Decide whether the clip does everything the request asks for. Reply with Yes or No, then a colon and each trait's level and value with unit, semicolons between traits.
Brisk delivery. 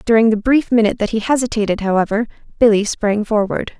No: average, 175 wpm